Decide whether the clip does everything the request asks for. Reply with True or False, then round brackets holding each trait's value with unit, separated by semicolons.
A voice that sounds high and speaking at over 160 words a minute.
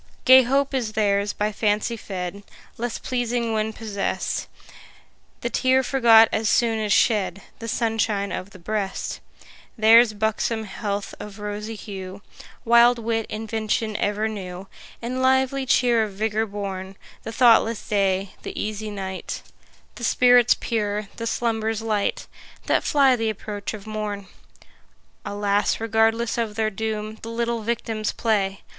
False (220 Hz; 140 wpm)